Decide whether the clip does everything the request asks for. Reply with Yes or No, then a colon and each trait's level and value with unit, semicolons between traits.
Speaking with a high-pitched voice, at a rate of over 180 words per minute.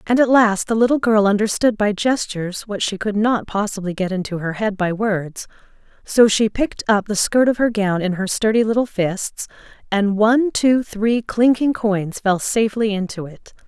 Yes: high, 210 Hz; average, 195 wpm